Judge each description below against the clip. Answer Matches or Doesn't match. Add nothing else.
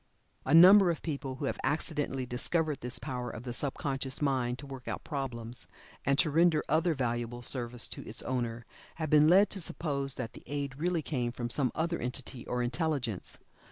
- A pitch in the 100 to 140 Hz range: Matches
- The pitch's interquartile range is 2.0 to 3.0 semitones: Doesn't match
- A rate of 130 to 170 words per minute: Doesn't match